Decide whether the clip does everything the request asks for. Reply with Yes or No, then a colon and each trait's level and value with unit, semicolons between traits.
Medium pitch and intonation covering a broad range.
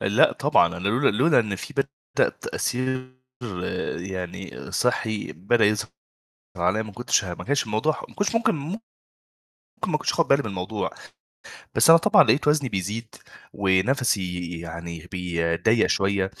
No: low, 105 Hz; wide, 6.2 semitones